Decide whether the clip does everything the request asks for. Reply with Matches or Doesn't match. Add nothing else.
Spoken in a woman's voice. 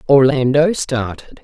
Matches